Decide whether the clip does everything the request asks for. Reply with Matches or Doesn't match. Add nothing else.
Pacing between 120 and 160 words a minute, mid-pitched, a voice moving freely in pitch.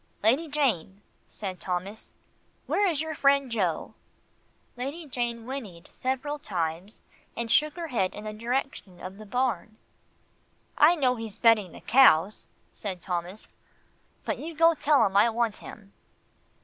Doesn't match